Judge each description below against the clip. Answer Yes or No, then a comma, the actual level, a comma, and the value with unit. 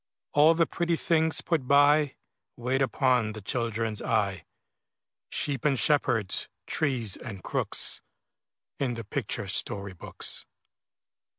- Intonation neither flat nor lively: Yes, average, 5.0 semitones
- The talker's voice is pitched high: No, low, 130 Hz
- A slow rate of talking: Yes, slow, 115 wpm